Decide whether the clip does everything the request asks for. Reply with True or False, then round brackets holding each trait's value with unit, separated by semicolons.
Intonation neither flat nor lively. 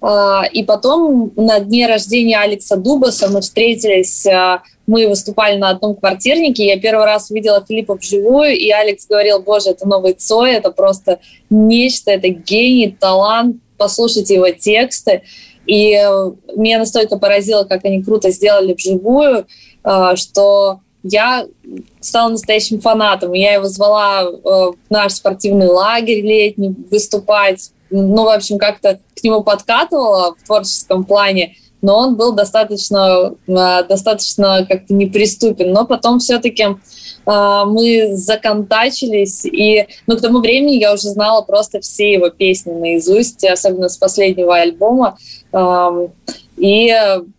False (2.3 semitones)